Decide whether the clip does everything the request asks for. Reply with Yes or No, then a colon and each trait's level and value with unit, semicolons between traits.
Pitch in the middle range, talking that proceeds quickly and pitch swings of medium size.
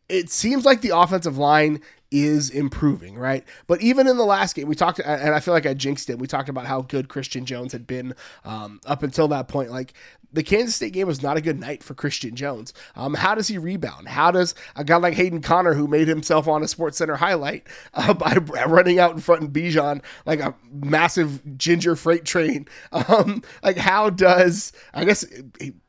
Yes: medium, 155 Hz; fast, 215 wpm; average, 3.9 semitones